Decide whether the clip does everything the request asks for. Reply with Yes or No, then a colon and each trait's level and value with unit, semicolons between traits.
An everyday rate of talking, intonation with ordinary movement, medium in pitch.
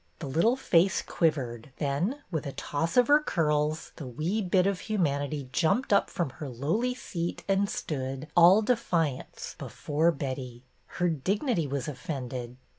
No: average, 150 wpm; wide, 5.9 semitones; medium, 160 Hz